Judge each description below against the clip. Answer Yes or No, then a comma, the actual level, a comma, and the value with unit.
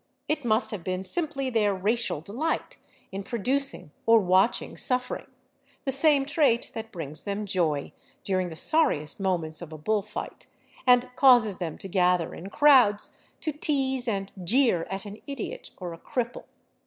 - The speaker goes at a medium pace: Yes, average, 160 wpm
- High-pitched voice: Yes, high, 215 Hz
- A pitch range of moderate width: No, wide, 5.9 semitones